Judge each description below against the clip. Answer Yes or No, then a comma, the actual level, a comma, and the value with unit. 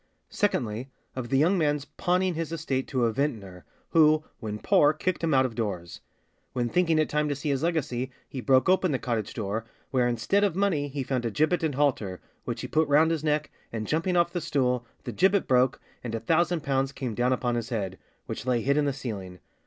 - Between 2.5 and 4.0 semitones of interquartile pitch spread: No, average, 4.9 semitones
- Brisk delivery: Yes, fast, 220 wpm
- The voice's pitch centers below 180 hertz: Yes, medium, 140 Hz